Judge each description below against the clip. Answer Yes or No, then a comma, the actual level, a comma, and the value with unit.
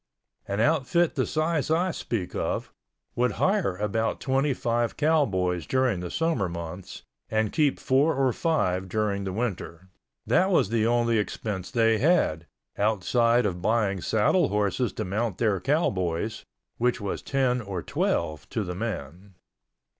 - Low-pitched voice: Yes, low, 110 Hz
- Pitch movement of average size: No, wide, 5.8 semitones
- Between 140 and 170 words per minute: Yes, average, 145 wpm